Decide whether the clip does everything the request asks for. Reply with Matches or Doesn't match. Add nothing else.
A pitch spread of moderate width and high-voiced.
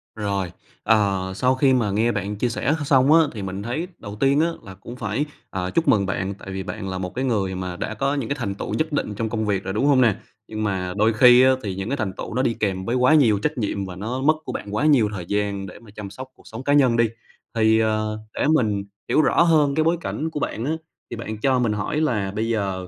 Doesn't match